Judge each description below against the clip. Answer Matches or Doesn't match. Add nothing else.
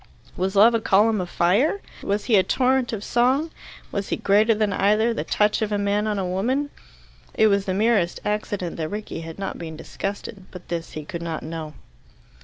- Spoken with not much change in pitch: Doesn't match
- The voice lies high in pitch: Matches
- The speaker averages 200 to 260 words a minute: Matches